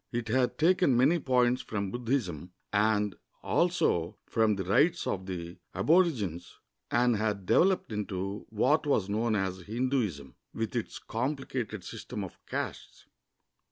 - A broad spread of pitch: No, average, 5.0 semitones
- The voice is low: Yes, low, 110 Hz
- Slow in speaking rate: Yes, slow, 130 wpm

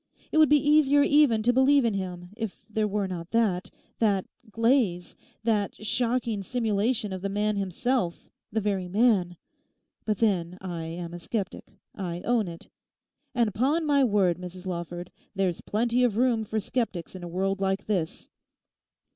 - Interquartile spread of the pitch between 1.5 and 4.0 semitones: No, average, 4.6 semitones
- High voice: Yes, high, 210 Hz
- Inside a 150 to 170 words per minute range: Yes, average, 160 wpm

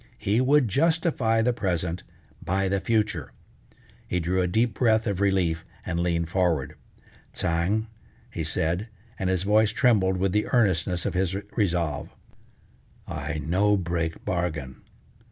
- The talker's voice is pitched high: No, very low, 95 Hz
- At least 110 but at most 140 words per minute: Yes, slow, 135 wpm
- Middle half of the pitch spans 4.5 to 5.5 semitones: No, average, 4.1 semitones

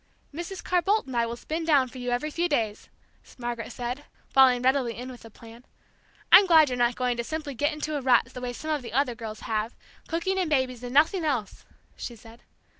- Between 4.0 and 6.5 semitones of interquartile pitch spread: Yes, average, 4.4 semitones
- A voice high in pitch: Yes, very high, 255 Hz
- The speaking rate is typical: No, fast, 225 wpm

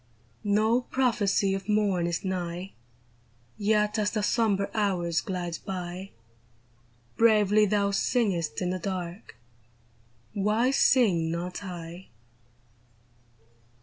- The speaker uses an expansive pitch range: No, average, 3.3 semitones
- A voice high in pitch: Yes, high, 195 Hz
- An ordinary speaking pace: No, slow, 105 wpm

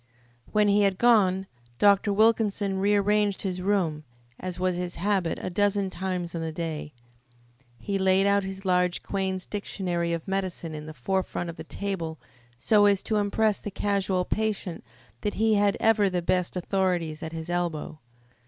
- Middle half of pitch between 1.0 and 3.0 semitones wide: Yes, average, 2.7 semitones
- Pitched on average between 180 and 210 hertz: Yes, high, 190 Hz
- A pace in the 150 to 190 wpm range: Yes, average, 165 wpm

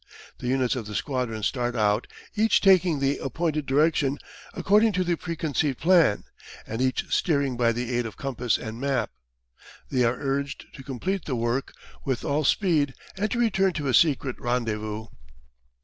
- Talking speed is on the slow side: No, average, 165 wpm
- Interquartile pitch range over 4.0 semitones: Yes, average, 5.0 semitones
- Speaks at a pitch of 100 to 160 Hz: Yes, low, 135 Hz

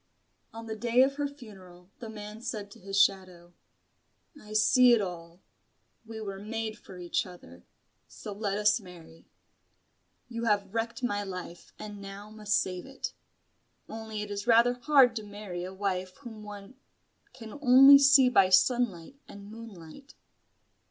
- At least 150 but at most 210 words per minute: Yes, average, 155 wpm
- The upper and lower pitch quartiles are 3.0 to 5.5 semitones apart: Yes, average, 3.6 semitones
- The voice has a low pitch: No, high, 210 Hz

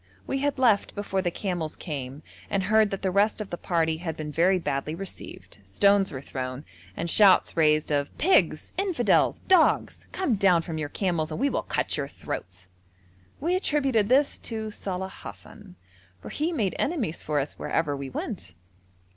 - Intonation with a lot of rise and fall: Yes, wide, 6.1 semitones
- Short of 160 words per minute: No, average, 175 wpm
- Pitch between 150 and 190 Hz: Yes, medium, 185 Hz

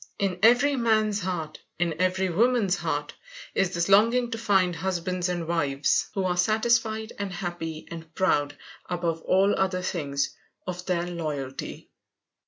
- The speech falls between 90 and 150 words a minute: Yes, average, 140 wpm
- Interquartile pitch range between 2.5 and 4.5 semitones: Yes, average, 3.3 semitones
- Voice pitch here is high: No, medium, 180 Hz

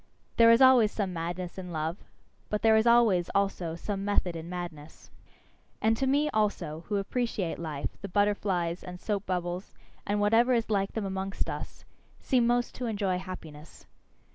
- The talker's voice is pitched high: Yes, high, 195 Hz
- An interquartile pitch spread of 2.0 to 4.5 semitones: Yes, average, 4.0 semitones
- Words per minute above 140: Yes, average, 165 wpm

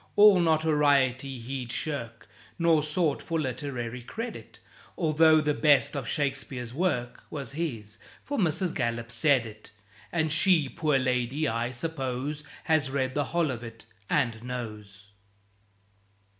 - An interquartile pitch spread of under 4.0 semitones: No, average, 4.5 semitones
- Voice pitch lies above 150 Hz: No, medium, 140 Hz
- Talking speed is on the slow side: Yes, slow, 130 wpm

